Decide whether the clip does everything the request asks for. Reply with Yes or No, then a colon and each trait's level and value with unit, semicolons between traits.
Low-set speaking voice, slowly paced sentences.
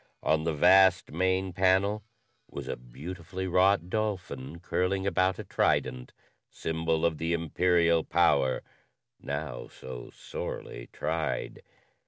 Yes: very low, 85 Hz; slow, 115 wpm